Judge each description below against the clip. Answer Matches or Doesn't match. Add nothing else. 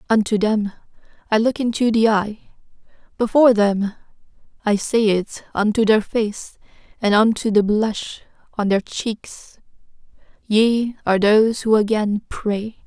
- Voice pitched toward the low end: Doesn't match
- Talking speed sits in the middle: Doesn't match